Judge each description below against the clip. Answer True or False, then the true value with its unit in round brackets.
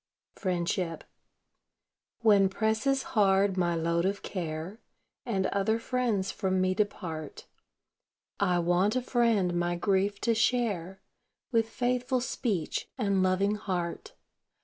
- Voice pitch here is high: True (195 Hz)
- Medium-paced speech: False (115 wpm)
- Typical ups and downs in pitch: True (3.8 semitones)